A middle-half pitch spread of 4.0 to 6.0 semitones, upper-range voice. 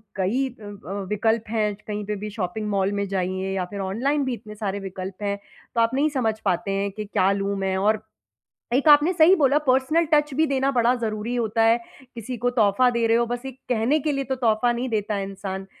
Yes: average, 4.3 semitones; high, 220 Hz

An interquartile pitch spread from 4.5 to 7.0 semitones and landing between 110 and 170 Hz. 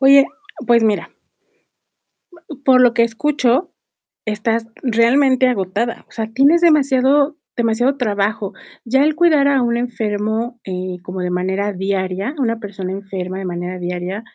No: average, 5.2 semitones; high, 230 Hz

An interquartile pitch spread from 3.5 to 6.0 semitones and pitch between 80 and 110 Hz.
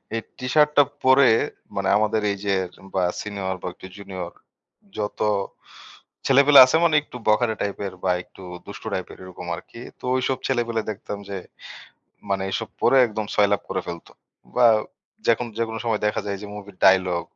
Yes: average, 3.9 semitones; low, 105 Hz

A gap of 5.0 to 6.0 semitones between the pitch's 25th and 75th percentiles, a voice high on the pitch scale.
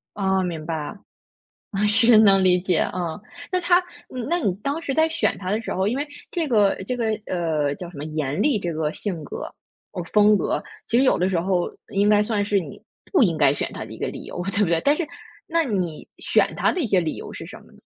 Yes: average, 5.3 semitones; high, 195 Hz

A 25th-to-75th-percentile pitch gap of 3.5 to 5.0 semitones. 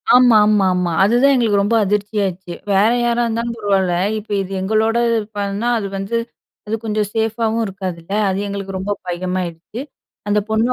No: average, 2.7 semitones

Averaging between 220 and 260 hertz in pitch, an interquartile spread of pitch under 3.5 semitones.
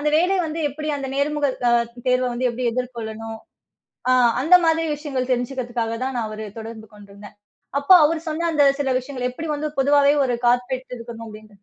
No: very high, 255 Hz; average, 4.1 semitones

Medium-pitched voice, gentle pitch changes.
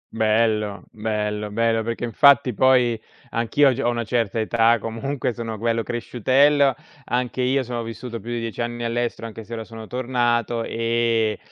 No: low, 115 Hz; narrow, 1.4 semitones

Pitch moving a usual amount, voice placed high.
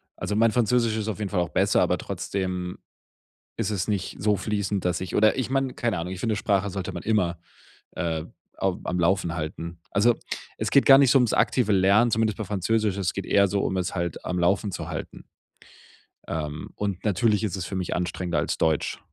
No: average, 3.4 semitones; low, 100 Hz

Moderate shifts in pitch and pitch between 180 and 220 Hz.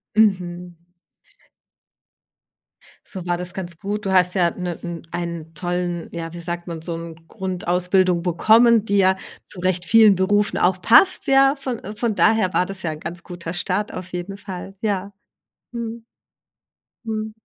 Yes: average, 3.0 semitones; medium, 185 Hz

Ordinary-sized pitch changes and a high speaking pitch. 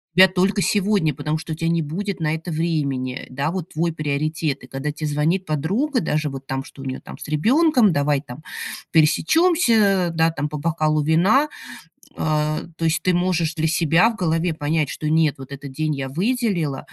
No: average, 3.6 semitones; medium, 160 Hz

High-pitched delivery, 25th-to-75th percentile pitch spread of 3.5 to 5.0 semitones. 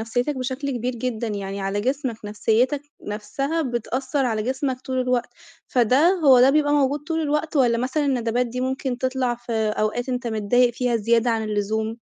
No: high, 245 Hz; average, 2.9 semitones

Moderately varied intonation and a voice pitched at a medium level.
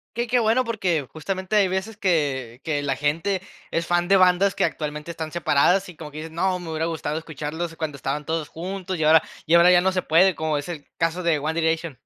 Yes: average, 3.3 semitones; medium, 165 Hz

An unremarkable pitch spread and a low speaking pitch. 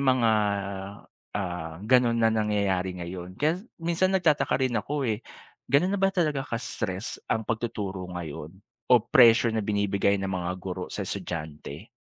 No: wide, 5.8 semitones; low, 105 Hz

